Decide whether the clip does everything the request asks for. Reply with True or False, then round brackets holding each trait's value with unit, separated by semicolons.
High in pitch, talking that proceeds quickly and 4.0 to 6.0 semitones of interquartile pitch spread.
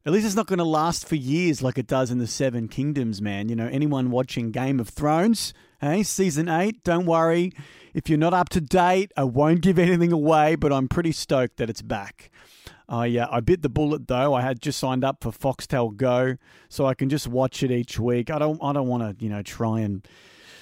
False (140 Hz; 240 wpm; 4.7 semitones)